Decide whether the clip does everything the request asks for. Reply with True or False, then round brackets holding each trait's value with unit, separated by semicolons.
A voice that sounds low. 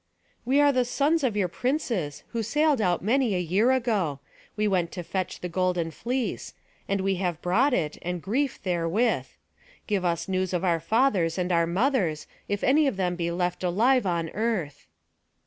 False (190 Hz)